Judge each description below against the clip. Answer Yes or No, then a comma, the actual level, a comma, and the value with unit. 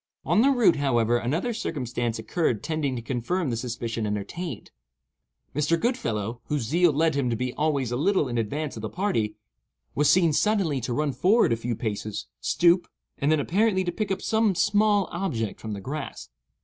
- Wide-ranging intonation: Yes, wide, 7.4 semitones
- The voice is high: No, medium, 145 Hz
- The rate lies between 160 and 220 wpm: Yes, average, 185 wpm